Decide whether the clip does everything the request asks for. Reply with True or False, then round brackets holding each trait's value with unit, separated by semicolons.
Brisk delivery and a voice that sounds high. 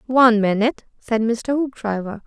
False (135 wpm; 230 Hz)